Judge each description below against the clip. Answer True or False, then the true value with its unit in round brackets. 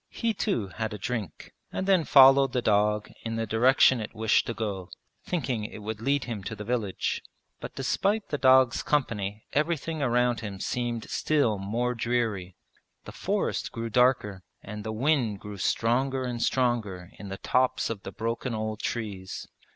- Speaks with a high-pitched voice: False (115 Hz)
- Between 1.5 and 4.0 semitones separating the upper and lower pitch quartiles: True (3.7 semitones)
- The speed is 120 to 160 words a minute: False (170 wpm)